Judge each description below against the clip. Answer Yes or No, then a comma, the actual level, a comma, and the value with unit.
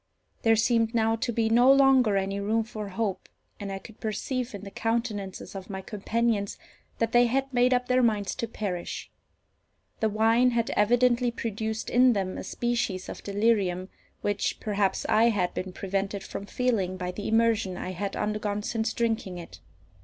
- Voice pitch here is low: No, high, 220 Hz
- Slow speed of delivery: No, average, 175 wpm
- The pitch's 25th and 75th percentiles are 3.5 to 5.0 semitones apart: No, average, 2.9 semitones